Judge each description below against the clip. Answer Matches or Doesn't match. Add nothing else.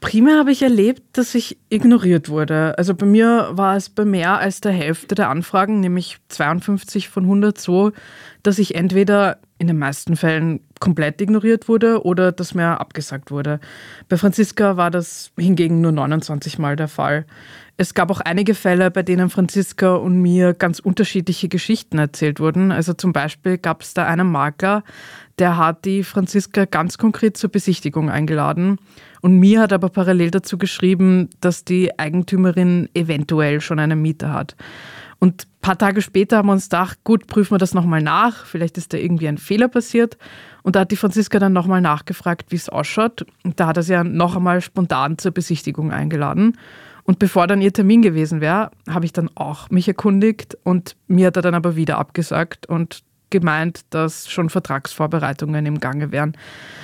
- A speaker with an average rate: Matches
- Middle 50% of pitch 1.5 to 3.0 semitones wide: Doesn't match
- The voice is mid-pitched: Matches